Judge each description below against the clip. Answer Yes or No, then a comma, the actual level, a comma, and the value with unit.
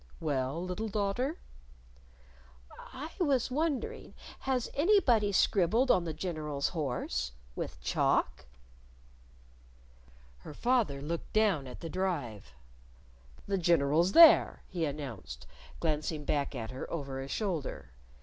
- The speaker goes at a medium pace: No, slow, 110 wpm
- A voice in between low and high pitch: Yes, medium, 170 Hz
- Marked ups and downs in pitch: Yes, wide, 8.0 semitones